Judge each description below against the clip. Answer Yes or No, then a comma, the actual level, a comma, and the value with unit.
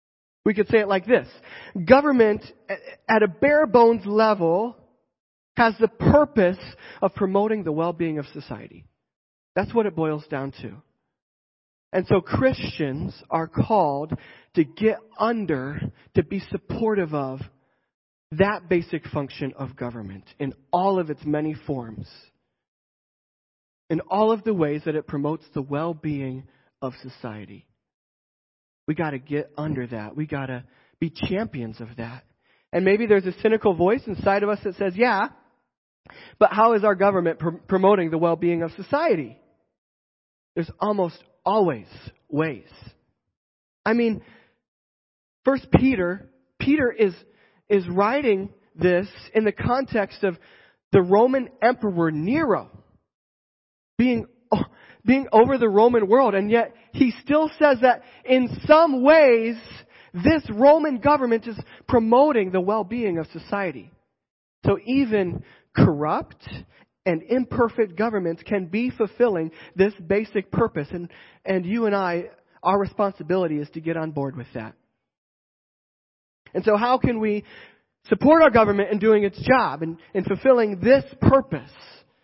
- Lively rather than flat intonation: Yes, wide, 6.7 semitones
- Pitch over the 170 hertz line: Yes, high, 190 Hz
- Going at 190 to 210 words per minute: No, average, 140 wpm